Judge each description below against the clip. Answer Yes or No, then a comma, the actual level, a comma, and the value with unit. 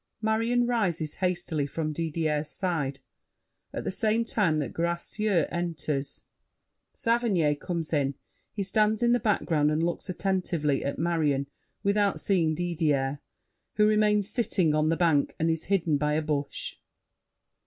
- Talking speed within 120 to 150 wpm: Yes, average, 140 wpm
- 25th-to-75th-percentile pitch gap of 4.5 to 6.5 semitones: Yes, average, 5.1 semitones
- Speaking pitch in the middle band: Yes, medium, 170 Hz